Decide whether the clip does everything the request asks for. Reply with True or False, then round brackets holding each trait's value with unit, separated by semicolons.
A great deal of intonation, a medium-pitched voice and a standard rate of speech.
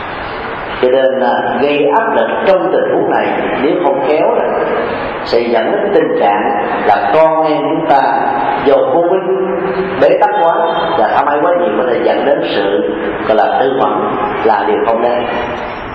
True (6.0 semitones; 155 Hz; 175 wpm)